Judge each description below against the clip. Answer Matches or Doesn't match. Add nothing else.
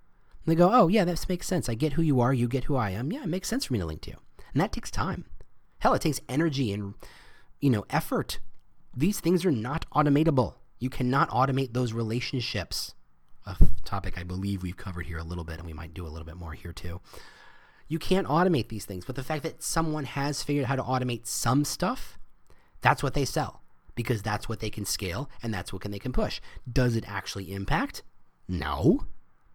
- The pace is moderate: Doesn't match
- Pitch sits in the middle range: Doesn't match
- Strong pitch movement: Matches